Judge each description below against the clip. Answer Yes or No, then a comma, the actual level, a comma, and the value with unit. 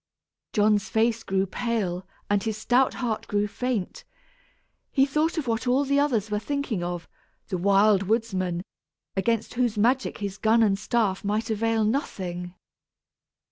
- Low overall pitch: No, high, 220 Hz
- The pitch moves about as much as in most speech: Yes, average, 3.6 semitones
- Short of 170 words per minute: Yes, average, 145 wpm